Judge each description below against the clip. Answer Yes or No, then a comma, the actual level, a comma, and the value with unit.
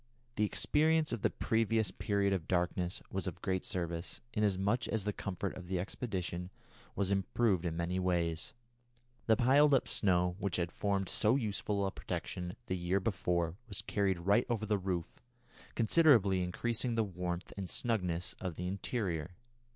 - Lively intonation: No, average, 3.5 semitones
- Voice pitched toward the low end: Yes, very low, 95 Hz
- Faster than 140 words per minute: Yes, average, 160 wpm